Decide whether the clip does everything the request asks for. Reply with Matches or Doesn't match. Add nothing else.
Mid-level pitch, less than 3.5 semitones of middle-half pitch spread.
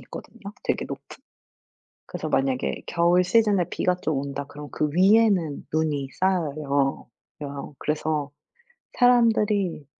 Doesn't match